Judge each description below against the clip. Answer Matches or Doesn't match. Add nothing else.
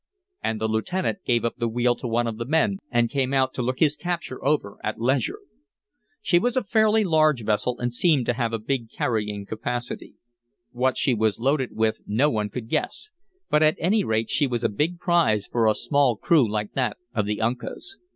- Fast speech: Matches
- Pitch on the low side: Matches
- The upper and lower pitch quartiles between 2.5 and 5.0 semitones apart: Doesn't match